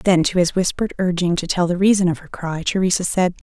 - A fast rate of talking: Yes, fast, 240 wpm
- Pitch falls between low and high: Yes, medium, 180 Hz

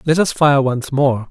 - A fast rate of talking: Yes, fast, 230 wpm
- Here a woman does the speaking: No, male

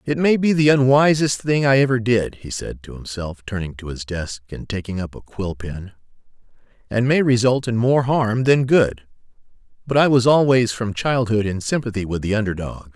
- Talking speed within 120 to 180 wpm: No, average, 200 wpm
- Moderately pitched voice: No, low, 115 Hz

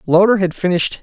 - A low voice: No, medium, 185 Hz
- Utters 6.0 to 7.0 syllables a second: Yes, 6.6 syllables/s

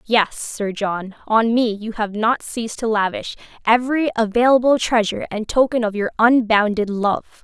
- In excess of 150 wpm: Yes, average, 160 wpm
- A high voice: Yes, high, 225 Hz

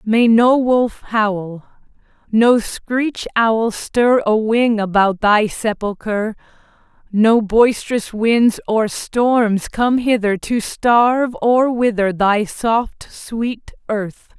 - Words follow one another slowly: Yes, slow, 115 wpm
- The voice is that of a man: No, female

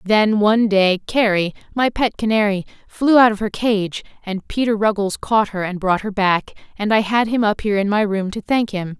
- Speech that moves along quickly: Yes, fast, 220 wpm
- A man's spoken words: No, female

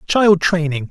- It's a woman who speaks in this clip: No, male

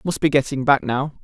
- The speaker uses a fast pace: Yes, fast, 245 wpm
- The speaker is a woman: No, male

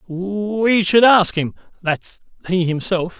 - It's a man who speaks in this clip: Yes, male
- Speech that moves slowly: Yes, slow, 130 wpm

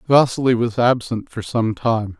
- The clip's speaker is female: No, male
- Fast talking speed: No, average, 165 wpm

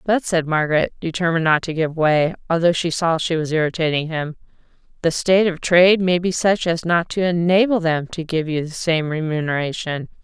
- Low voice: No, medium, 165 Hz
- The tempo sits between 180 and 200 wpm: Yes, average, 195 wpm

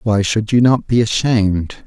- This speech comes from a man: Yes, male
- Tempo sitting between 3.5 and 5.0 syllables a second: Yes, 4.5 syllables/s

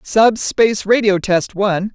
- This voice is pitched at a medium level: No, high, 205 Hz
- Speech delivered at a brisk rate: No, slow, 125 wpm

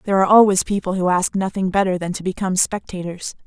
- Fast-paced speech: Yes, fast, 210 wpm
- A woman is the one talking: Yes, female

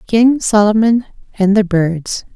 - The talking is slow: Yes, slow, 130 wpm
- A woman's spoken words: Yes, female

